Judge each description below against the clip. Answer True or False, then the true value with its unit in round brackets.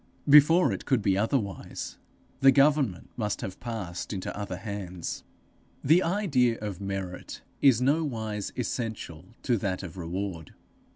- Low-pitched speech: True (105 Hz)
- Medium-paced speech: False (130 wpm)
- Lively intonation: True (5.9 semitones)